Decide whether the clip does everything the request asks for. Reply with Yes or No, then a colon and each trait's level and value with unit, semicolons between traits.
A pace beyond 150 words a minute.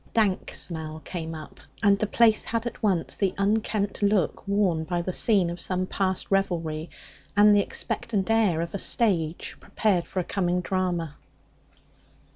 Yes: average, 165 wpm